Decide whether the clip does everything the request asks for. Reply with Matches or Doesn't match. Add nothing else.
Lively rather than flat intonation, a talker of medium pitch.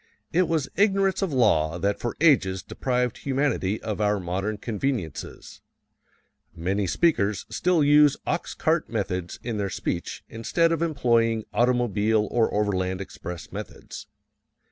Doesn't match